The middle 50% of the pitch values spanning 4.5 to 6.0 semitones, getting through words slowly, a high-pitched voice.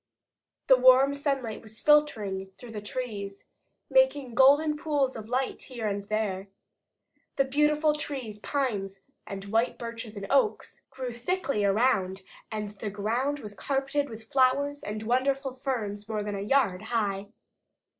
No: average, 4.9 semitones; average, 145 wpm; high, 240 Hz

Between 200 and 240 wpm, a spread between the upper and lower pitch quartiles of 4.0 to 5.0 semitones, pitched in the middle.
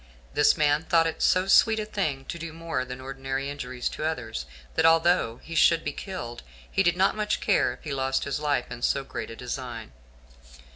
Yes: fast, 205 wpm; average, 4.3 semitones; medium, 145 Hz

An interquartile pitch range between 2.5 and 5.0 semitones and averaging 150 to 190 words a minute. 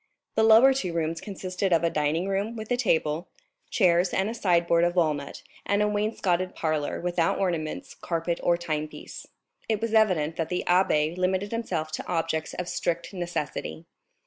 Yes: average, 3.4 semitones; average, 170 wpm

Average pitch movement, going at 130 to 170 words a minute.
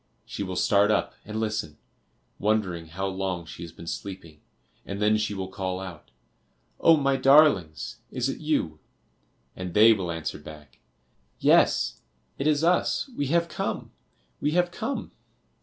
No: wide, 7.8 semitones; average, 155 wpm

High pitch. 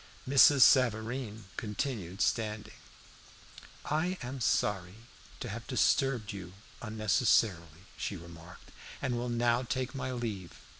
No: low, 115 Hz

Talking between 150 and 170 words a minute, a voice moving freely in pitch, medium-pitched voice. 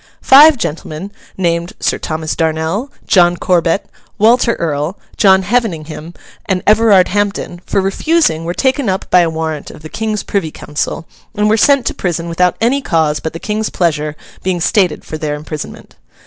No: average, 165 wpm; average, 4.8 semitones; medium, 180 Hz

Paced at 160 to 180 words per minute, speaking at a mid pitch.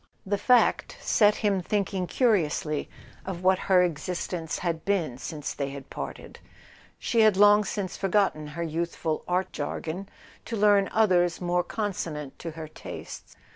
No: average, 145 wpm; medium, 180 Hz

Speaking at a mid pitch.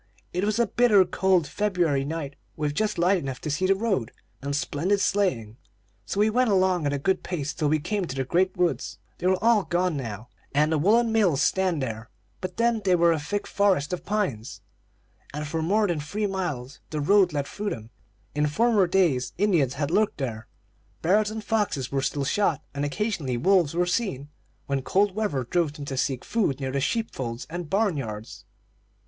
Yes: medium, 170 Hz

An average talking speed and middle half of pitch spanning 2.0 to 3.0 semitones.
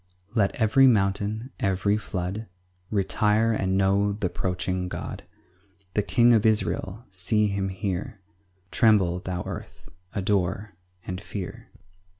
No: slow, 125 wpm; narrow, 2.4 semitones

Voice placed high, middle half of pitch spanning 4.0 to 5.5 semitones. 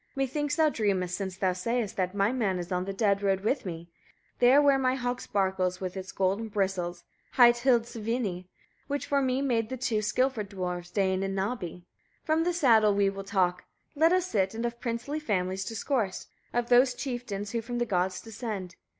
Yes: high, 215 Hz; average, 4.7 semitones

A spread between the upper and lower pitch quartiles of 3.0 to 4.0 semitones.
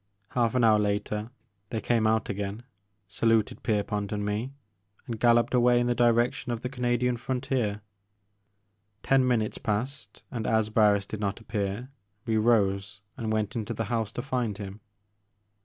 No: narrow, 2.6 semitones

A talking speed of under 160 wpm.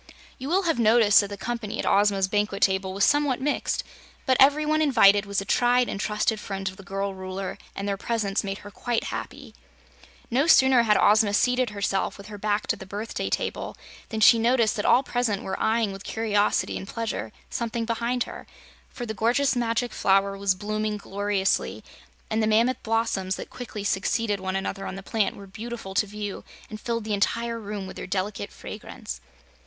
No: average, 195 wpm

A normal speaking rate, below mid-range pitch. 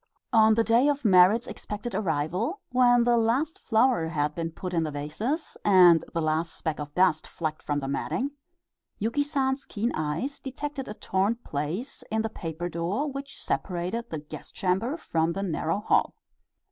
No: average, 170 wpm; high, 200 Hz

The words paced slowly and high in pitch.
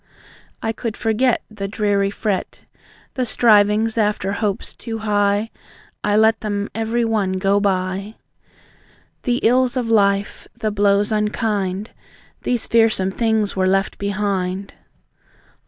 Yes: slow, 120 wpm; high, 210 Hz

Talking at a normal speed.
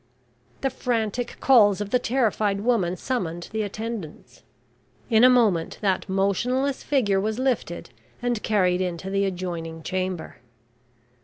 No: slow, 130 wpm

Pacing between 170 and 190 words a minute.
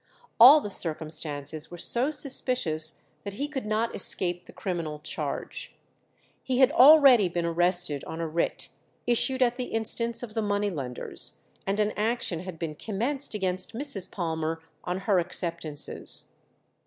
No: average, 150 wpm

